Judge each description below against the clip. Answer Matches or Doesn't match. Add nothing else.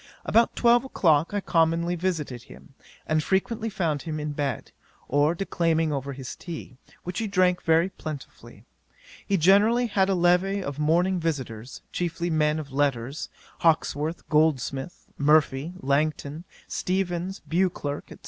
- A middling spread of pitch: Matches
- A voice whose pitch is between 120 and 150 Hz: Doesn't match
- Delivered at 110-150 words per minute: Matches